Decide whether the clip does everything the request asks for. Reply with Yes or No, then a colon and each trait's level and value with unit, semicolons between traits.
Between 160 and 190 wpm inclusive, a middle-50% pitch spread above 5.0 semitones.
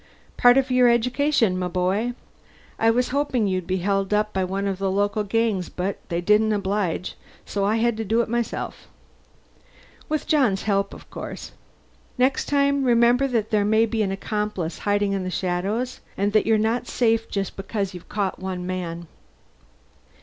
No: average, 170 wpm; average, 3.6 semitones